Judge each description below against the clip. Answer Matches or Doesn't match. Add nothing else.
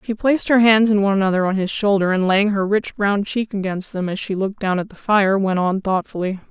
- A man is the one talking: Doesn't match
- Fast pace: Matches